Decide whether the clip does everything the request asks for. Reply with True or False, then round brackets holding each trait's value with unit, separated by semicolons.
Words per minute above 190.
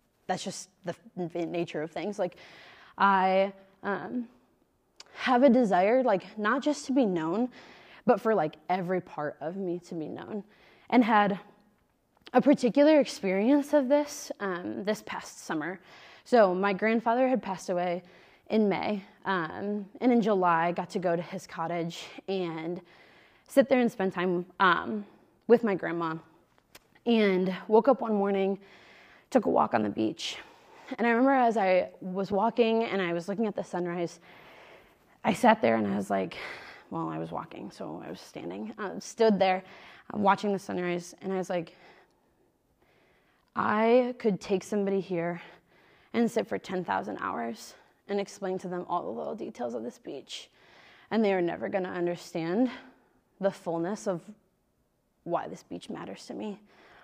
False (165 wpm)